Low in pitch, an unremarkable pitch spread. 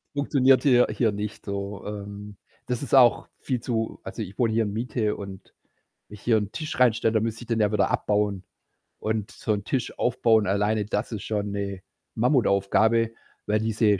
No: low, 110 Hz; narrow, 2.3 semitones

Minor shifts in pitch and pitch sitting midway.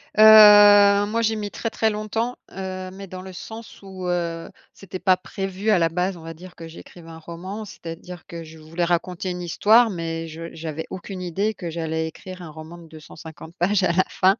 No: average, 3.4 semitones; medium, 180 Hz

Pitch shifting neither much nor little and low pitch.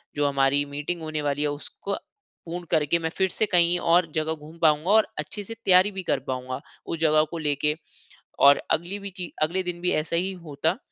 No: average, 3.2 semitones; medium, 160 Hz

